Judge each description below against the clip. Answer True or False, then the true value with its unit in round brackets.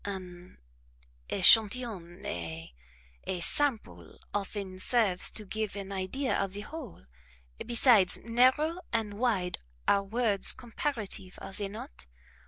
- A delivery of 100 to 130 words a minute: True (115 wpm)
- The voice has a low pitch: False (205 Hz)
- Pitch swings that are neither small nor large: True (4.1 semitones)